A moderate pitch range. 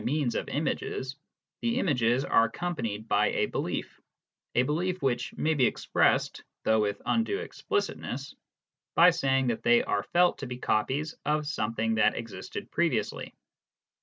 No: wide, 5.8 semitones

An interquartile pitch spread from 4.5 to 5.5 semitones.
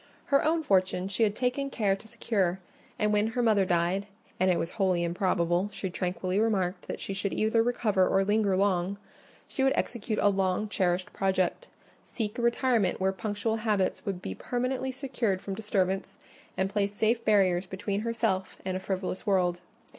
No: average, 3.0 semitones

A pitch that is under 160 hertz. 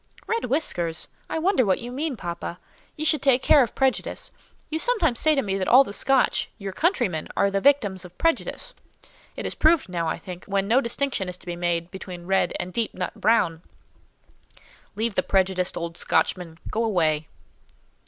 No: high, 200 Hz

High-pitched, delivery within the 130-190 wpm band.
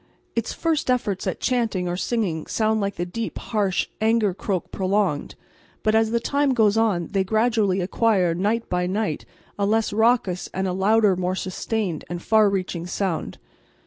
Yes: high, 205 Hz; average, 170 wpm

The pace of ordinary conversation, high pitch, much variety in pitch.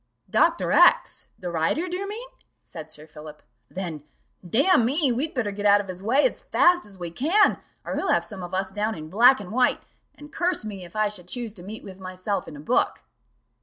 No: fast, 220 wpm; high, 205 Hz; wide, 6.2 semitones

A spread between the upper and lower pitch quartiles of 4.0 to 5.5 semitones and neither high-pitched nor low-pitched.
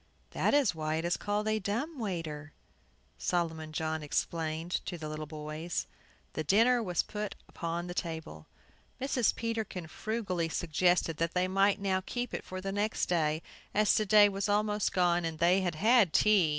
Yes: average, 4.5 semitones; medium, 180 Hz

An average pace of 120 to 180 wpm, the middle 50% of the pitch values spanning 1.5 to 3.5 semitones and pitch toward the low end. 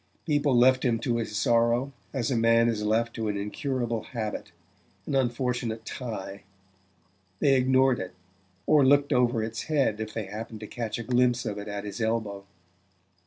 Yes: average, 170 wpm; average, 2.8 semitones; low, 115 Hz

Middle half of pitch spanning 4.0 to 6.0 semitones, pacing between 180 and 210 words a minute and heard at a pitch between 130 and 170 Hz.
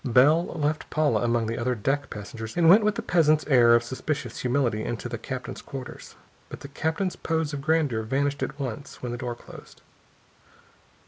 Yes: average, 4.5 semitones; average, 185 wpm; low, 135 Hz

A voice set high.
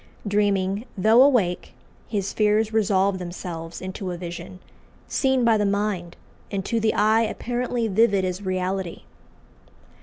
Yes: high, 200 Hz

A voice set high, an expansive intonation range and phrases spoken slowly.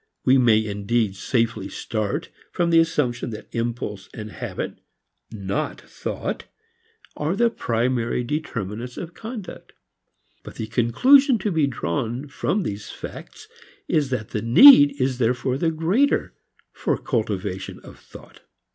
No: low, 125 Hz; wide, 6.4 semitones; slow, 130 wpm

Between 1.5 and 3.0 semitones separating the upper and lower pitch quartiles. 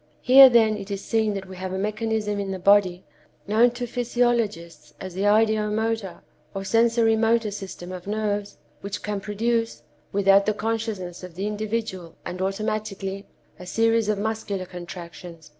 Yes: average, 2.7 semitones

